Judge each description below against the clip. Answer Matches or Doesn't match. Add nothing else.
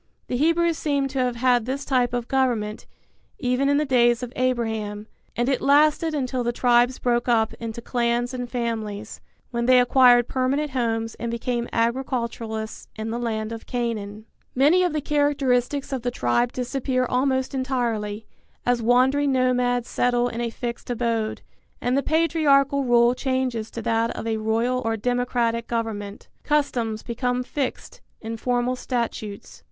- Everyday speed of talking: Matches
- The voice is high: Matches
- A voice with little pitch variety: Matches